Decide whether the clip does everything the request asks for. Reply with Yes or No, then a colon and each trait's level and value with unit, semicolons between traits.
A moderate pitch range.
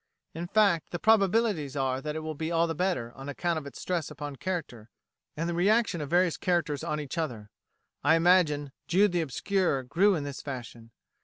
Yes: average, 4.0 semitones